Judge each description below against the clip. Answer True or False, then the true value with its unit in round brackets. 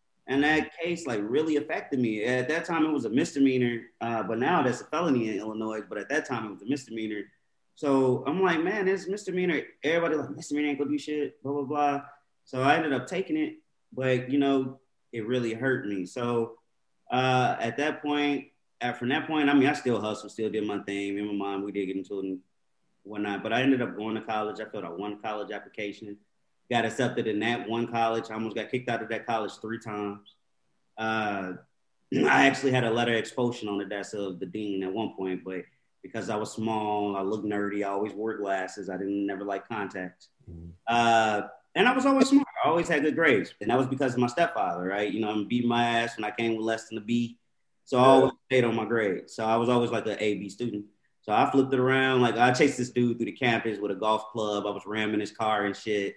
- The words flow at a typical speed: False (240 wpm)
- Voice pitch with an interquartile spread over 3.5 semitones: True (4.3 semitones)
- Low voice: True (115 Hz)